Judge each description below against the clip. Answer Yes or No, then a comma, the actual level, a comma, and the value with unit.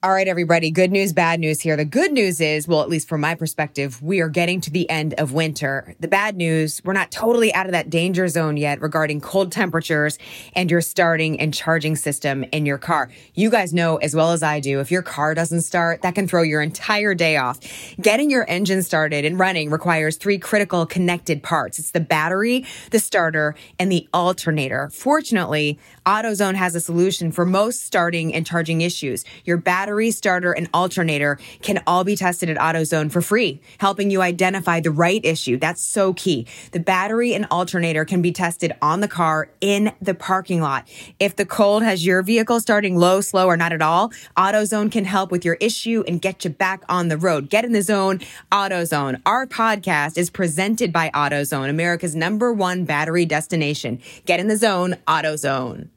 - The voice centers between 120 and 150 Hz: No, medium, 175 Hz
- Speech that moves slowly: No, average, 195 wpm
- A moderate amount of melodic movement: Yes, average, 3.5 semitones